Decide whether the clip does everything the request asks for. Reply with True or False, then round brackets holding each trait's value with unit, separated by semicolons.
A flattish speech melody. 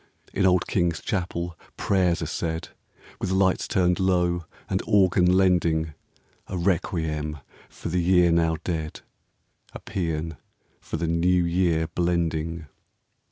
True (1.8 semitones)